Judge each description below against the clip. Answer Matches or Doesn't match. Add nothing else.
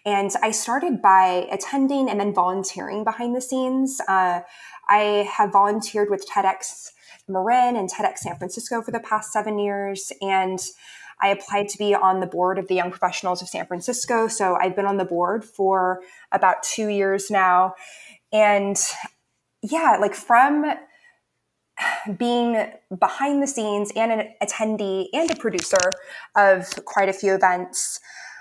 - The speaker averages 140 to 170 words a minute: Matches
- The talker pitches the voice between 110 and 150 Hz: Doesn't match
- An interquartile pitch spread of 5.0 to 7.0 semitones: Doesn't match